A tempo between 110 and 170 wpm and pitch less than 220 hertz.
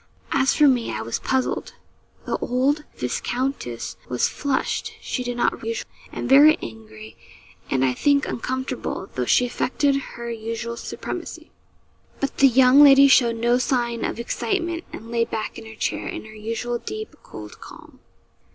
No: average, 160 wpm; high, 240 Hz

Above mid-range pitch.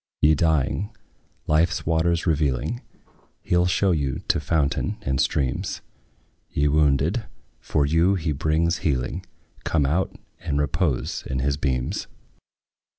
No: very low, 75 Hz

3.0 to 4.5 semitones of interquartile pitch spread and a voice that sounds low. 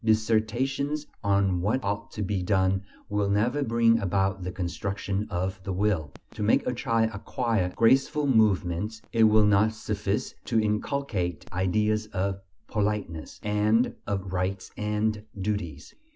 No: narrow, 2.5 semitones; low, 105 Hz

